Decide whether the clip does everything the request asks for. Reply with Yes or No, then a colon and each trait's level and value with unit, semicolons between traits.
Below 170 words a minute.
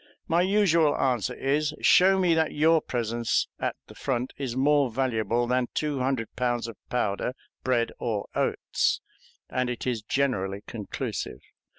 Yes: average, 150 wpm